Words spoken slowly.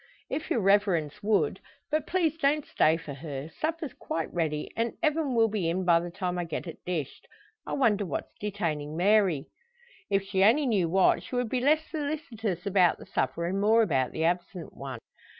No: average, 190 wpm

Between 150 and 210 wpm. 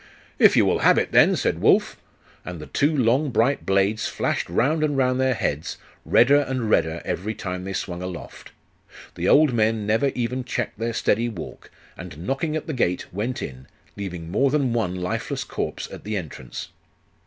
Yes: average, 185 wpm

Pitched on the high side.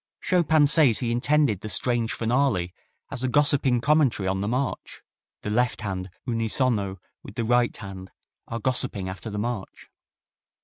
No: low, 120 Hz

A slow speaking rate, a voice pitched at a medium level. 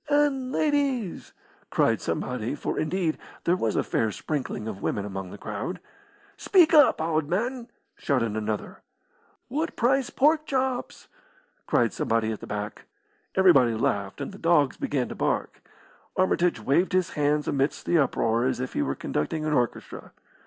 No: average, 155 wpm; medium, 155 Hz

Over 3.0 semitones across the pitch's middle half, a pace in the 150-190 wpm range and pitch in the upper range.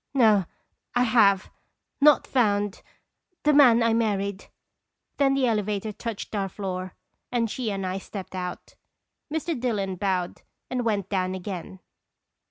No: average, 3.9 semitones; slow, 135 wpm; high, 205 Hz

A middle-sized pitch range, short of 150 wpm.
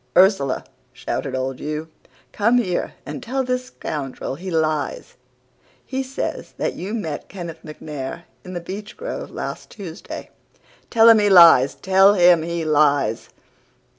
No: wide, 5.7 semitones; slow, 135 wpm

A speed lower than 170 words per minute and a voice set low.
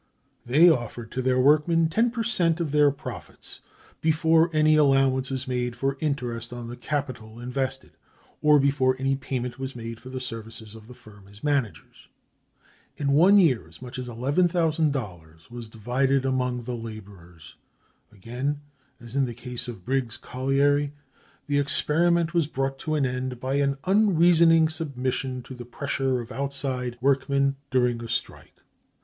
Yes: average, 160 wpm; low, 130 Hz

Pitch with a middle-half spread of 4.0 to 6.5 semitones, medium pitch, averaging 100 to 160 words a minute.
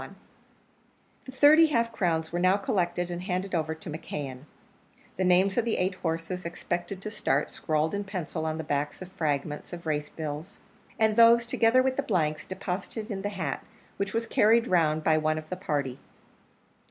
No: average, 4.6 semitones; medium, 180 Hz; average, 180 wpm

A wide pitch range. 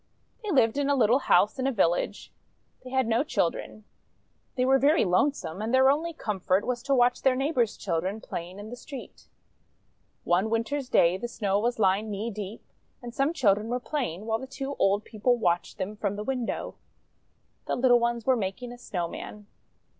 No: average, 4.4 semitones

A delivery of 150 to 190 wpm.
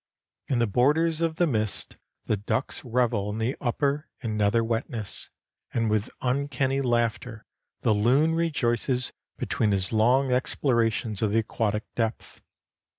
No: average, 140 wpm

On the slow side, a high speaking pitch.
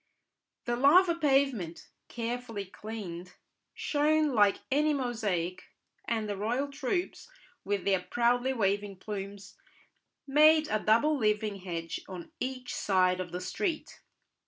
Yes: slow, 120 wpm; high, 225 Hz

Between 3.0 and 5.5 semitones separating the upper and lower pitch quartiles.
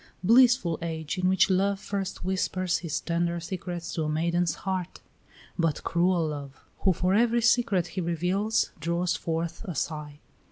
No: narrow, 2.4 semitones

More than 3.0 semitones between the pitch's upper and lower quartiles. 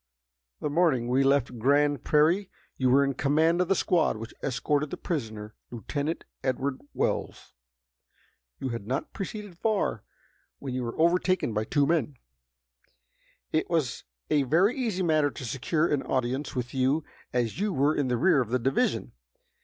Yes: average, 4.4 semitones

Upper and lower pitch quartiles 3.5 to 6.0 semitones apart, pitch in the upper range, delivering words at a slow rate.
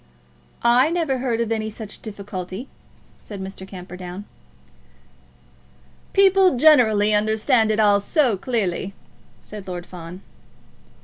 Yes: average, 4.3 semitones; high, 215 Hz; slow, 110 wpm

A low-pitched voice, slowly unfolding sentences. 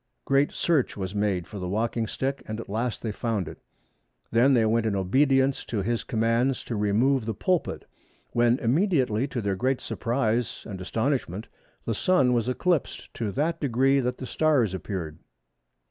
No: low, 120 Hz; average, 170 wpm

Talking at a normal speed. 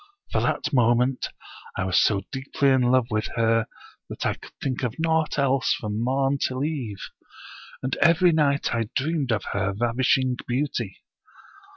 Yes: average, 160 wpm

